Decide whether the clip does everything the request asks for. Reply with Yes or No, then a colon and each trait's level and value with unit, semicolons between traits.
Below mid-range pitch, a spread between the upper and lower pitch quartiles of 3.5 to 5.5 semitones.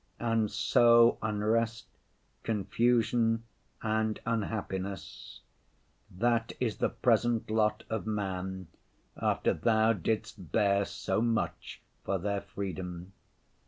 No: low, 110 Hz; narrow, 2.5 semitones